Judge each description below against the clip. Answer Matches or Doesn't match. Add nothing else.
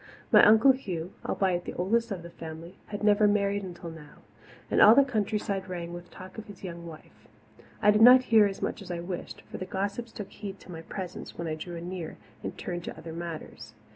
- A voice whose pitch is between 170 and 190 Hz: Matches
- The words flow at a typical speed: Doesn't match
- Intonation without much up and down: Doesn't match